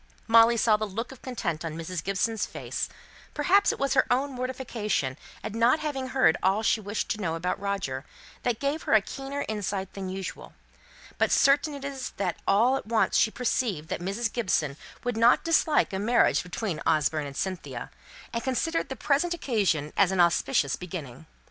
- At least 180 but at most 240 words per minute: Yes, average, 185 wpm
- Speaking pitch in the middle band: No, high, 220 Hz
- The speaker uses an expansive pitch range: Yes, wide, 6.1 semitones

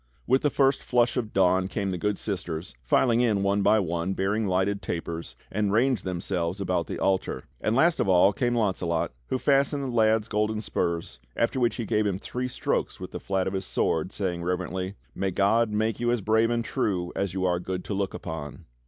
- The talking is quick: Yes, fast, 210 wpm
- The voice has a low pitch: Yes, low, 100 Hz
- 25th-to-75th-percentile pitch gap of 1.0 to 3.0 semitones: No, average, 3.7 semitones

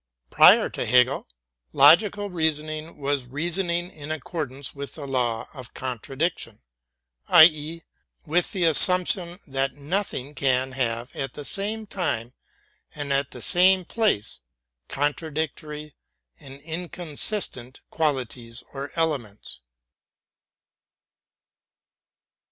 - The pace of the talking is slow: Yes, slow, 105 wpm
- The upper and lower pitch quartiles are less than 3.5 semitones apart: No, average, 4.3 semitones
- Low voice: No, medium, 150 Hz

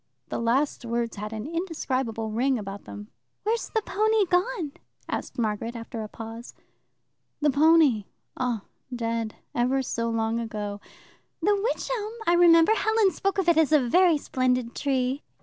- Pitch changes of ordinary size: No, wide, 7.1 semitones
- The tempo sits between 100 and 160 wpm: Yes, average, 155 wpm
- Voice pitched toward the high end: Yes, very high, 255 Hz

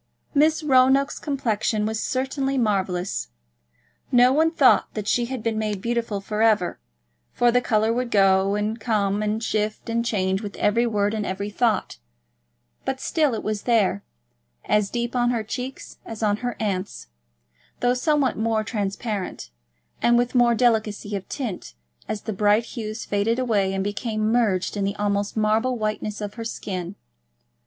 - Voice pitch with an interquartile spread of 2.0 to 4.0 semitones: Yes, average, 2.8 semitones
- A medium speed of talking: Yes, average, 165 wpm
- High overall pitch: Yes, high, 220 Hz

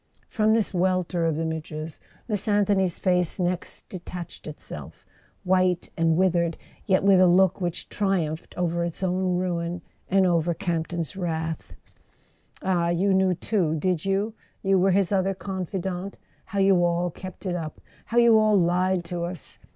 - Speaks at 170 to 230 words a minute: No, average, 150 wpm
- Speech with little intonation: Yes, narrow, 2.0 semitones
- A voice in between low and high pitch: Yes, medium, 180 Hz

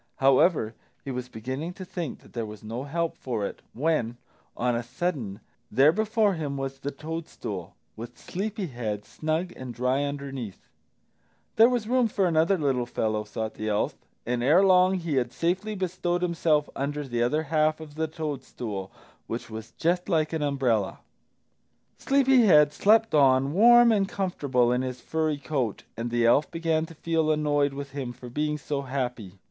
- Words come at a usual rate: Yes, average, 175 wpm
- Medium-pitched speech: Yes, medium, 145 Hz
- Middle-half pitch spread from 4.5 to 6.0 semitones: Yes, wide, 5.5 semitones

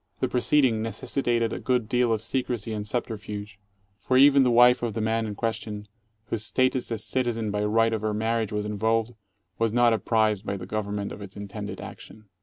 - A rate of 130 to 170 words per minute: No, average, 195 wpm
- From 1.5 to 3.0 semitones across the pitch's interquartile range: Yes, narrow, 2.4 semitones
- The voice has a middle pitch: No, low, 110 Hz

